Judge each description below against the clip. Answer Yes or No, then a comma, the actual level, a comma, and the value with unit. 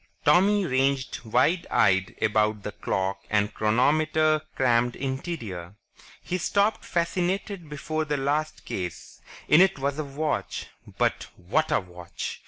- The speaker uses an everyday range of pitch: No, wide, 6.7 semitones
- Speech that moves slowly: Yes, slow, 130 wpm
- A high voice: No, medium, 140 Hz